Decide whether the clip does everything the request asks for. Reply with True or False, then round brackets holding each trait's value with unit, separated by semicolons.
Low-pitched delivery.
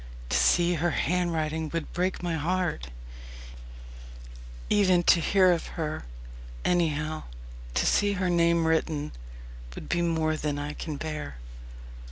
False (165 Hz)